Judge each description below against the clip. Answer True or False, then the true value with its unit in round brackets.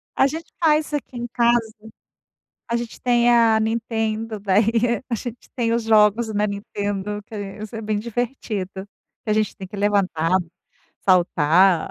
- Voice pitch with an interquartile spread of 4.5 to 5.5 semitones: False (2.6 semitones)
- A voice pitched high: True (220 Hz)